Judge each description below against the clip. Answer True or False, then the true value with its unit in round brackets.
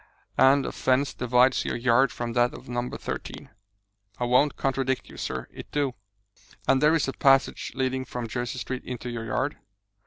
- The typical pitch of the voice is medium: False (130 Hz)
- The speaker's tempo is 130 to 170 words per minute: False (180 wpm)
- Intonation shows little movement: True (1.7 semitones)